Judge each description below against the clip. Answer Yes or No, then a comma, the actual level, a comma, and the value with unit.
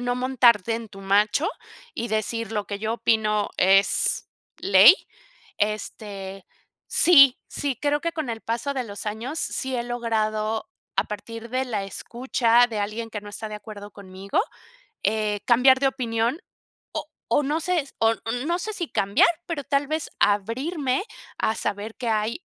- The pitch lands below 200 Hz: No, high, 230 Hz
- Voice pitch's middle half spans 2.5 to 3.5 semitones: No, average, 3.9 semitones